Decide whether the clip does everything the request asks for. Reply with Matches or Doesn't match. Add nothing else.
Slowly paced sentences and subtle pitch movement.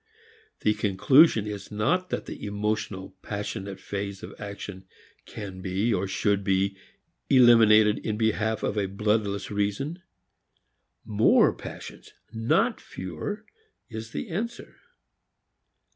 Matches